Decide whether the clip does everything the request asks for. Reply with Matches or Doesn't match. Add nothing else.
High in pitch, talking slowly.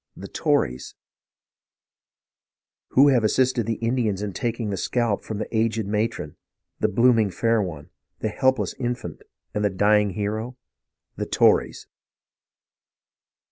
Doesn't match